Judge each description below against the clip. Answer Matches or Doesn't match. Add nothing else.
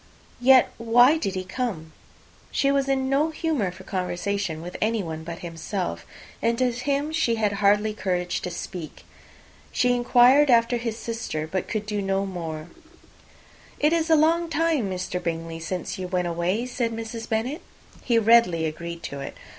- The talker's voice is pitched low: Doesn't match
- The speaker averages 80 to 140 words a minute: Doesn't match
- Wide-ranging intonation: Matches